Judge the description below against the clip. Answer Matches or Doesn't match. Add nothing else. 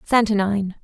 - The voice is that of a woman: Matches